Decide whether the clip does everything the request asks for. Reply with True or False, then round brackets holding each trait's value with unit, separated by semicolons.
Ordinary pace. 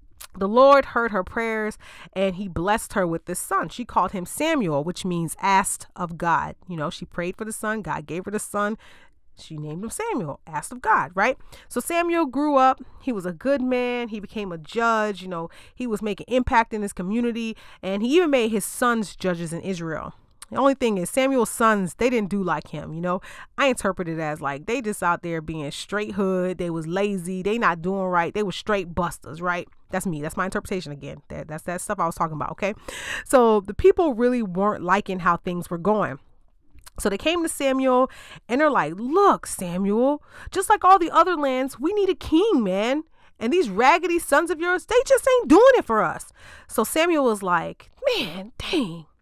False (210 wpm)